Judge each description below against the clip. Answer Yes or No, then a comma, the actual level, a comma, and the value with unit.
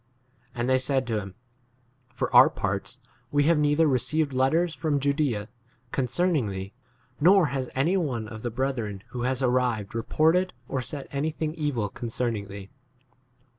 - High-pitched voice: No, low, 130 Hz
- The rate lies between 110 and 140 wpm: No, average, 160 wpm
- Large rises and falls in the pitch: No, average, 4.7 semitones